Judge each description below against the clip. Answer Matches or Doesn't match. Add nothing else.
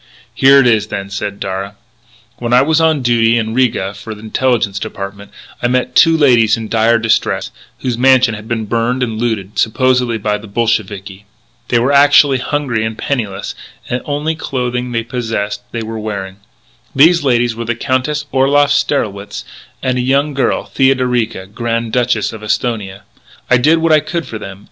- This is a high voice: Doesn't match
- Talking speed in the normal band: Matches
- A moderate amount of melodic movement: Matches